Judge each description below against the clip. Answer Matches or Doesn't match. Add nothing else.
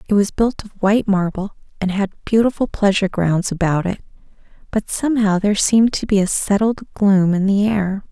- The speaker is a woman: Matches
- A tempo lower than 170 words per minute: Doesn't match